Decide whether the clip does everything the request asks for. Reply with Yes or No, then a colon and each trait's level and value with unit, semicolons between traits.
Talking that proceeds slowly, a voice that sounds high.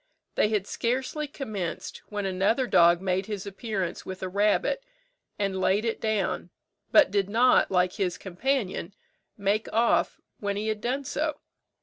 No: average, 150 wpm; high, 205 Hz